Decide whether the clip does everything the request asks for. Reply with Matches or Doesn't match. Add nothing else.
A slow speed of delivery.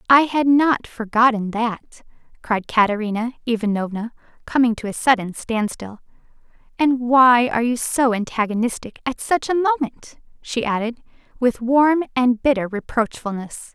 Matches